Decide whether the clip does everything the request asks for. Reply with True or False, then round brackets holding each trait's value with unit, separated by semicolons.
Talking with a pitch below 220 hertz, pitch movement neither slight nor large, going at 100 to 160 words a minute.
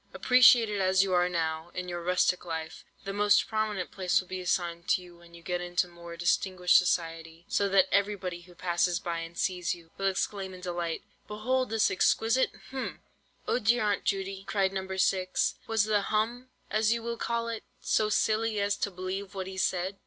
False (190 Hz; 3.1 semitones; 190 wpm)